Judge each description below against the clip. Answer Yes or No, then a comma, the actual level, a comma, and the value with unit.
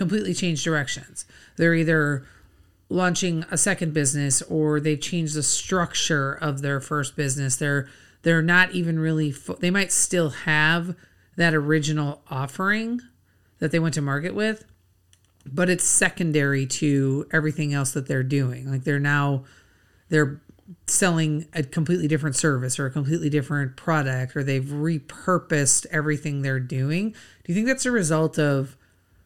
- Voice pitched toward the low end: No, medium, 150 Hz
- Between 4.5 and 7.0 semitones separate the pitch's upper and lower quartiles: No, average, 3.3 semitones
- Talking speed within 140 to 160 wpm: Yes, average, 150 wpm